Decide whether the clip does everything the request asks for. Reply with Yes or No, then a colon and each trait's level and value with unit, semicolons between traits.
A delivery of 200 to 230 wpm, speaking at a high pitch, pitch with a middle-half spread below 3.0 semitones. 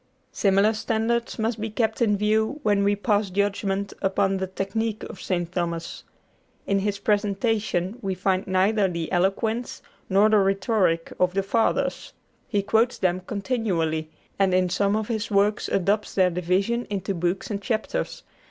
No: average, 155 wpm; high, 200 Hz; narrow, 2.5 semitones